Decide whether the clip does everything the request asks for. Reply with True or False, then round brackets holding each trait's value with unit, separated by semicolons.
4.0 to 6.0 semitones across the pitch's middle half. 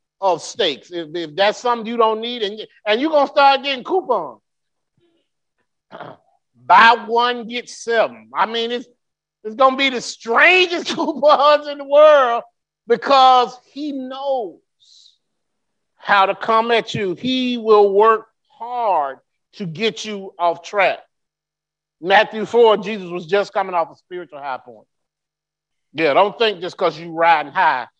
True (5.5 semitones)